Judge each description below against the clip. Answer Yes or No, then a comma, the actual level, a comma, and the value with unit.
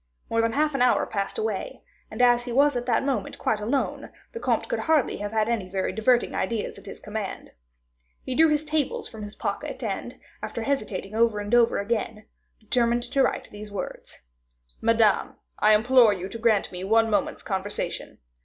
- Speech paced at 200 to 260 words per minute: No, average, 190 wpm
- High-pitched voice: Yes, high, 230 Hz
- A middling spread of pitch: Yes, average, 3.4 semitones